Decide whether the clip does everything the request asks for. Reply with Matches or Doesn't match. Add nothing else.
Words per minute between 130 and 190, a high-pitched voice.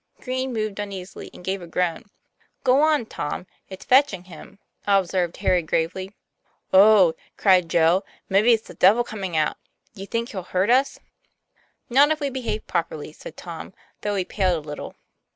Matches